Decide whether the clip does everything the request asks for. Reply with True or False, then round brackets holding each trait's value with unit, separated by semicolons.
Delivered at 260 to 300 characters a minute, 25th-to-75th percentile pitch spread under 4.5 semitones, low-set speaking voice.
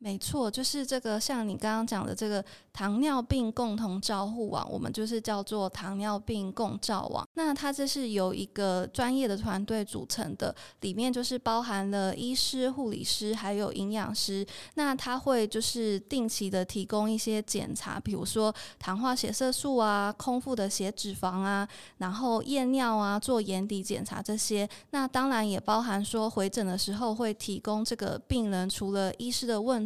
False (265 characters per minute; 3.6 semitones; 215 Hz)